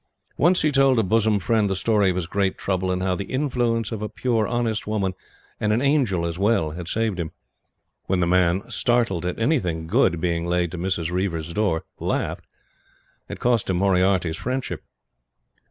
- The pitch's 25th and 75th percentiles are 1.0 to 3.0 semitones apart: No, average, 4.3 semitones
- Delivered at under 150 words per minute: No, average, 185 wpm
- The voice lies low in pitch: Yes, very low, 95 Hz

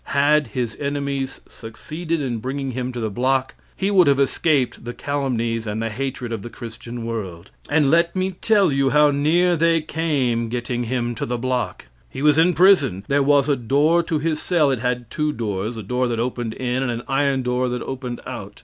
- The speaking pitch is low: Yes, low, 130 Hz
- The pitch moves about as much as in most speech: Yes, average, 3.8 semitones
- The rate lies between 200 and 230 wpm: Yes, fast, 205 wpm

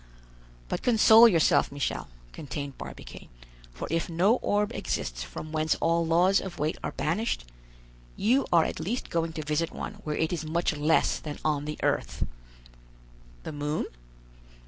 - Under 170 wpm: Yes, average, 155 wpm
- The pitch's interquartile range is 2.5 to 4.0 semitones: Yes, average, 2.9 semitones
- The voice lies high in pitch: No, medium, 160 Hz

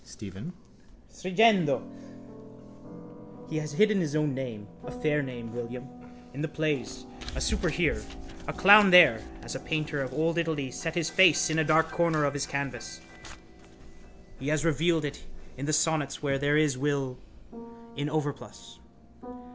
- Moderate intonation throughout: Yes, average, 3.2 semitones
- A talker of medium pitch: Yes, medium, 150 Hz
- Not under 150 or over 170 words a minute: Yes, average, 155 wpm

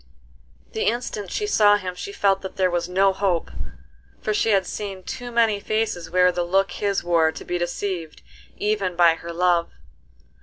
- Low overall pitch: No, high, 190 Hz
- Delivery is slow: No, average, 180 wpm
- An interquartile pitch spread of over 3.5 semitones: No, average, 2.9 semitones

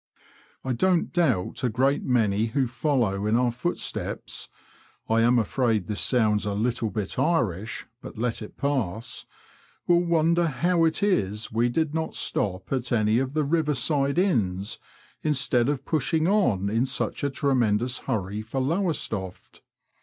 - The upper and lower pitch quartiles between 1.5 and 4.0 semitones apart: No, wide, 5.6 semitones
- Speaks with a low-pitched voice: Yes, low, 125 Hz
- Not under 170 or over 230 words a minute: No, average, 155 wpm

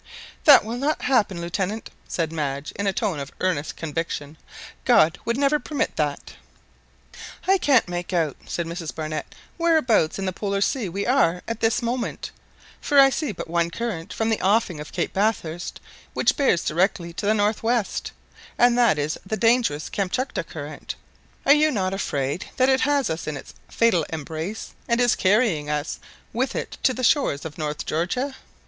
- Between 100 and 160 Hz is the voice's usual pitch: No, high, 195 Hz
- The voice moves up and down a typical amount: No, wide, 6.8 semitones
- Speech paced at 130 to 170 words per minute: No, average, 180 wpm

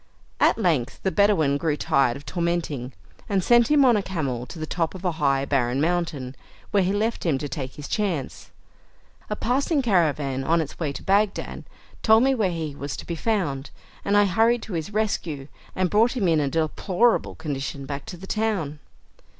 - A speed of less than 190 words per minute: No, average, 195 wpm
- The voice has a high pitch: No, medium, 170 Hz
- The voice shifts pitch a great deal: Yes, wide, 6.4 semitones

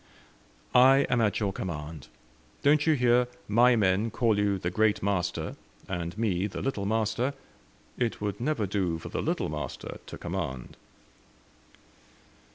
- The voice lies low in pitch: Yes, low, 105 Hz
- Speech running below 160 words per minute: Yes, average, 145 wpm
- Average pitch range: Yes, average, 4.6 semitones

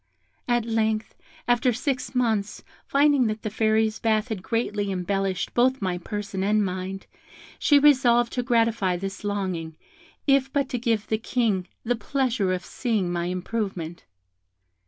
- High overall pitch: Yes, high, 220 Hz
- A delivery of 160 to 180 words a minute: No, average, 145 wpm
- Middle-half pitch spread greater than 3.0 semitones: Yes, average, 4.0 semitones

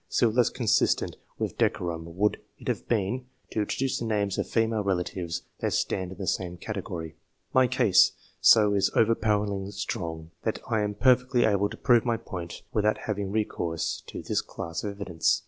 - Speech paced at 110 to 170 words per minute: No, average, 180 wpm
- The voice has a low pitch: Yes, low, 105 Hz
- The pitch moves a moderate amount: Yes, average, 3.8 semitones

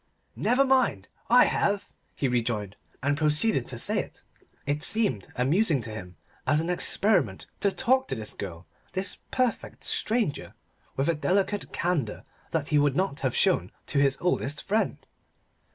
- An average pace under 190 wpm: Yes, average, 155 wpm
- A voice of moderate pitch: Yes, medium, 155 Hz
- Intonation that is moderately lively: No, wide, 7.8 semitones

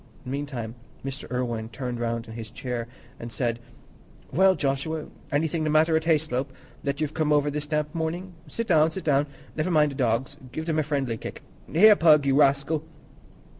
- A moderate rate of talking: Yes, average, 175 wpm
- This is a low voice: No, medium, 145 Hz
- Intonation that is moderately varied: Yes, average, 3.8 semitones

